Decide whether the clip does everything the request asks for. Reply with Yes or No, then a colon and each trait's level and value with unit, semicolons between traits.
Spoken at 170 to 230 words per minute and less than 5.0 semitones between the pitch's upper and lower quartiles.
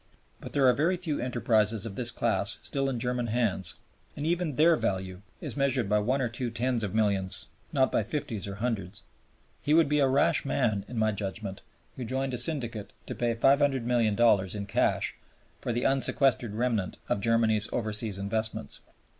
Yes: average, 180 wpm; average, 4.0 semitones